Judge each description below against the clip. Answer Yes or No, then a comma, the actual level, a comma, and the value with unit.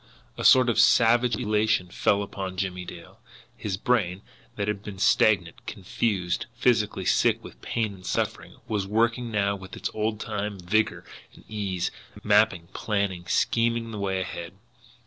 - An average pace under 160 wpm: Yes, average, 150 wpm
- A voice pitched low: Yes, low, 105 Hz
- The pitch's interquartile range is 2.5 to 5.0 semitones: Yes, average, 2.9 semitones